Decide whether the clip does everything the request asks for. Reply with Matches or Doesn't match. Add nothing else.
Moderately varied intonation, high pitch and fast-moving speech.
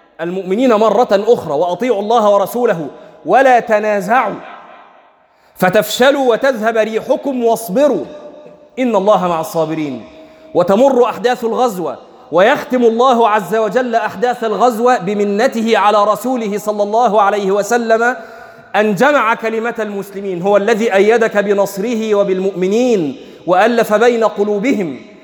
Doesn't match